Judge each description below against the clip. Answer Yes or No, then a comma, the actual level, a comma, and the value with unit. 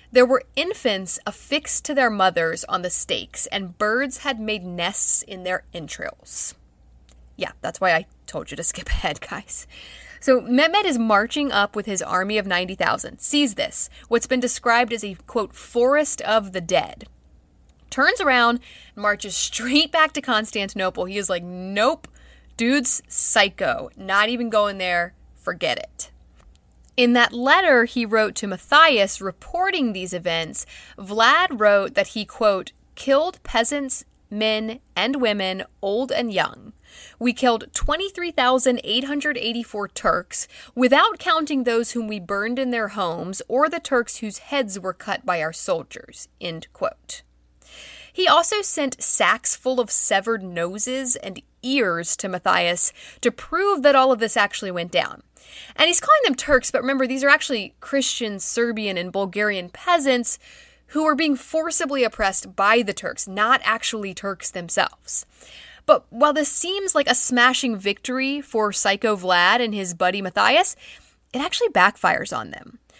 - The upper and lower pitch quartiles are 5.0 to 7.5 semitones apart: Yes, wide, 5.5 semitones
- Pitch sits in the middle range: No, high, 230 Hz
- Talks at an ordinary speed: Yes, average, 150 wpm